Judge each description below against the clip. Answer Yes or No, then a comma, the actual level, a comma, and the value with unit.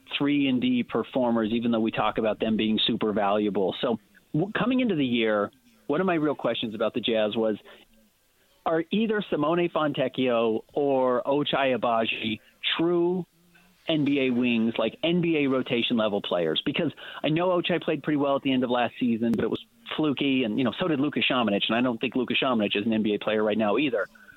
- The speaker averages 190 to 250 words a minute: Yes, average, 195 wpm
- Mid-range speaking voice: No, low, 130 Hz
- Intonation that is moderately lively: No, wide, 6.9 semitones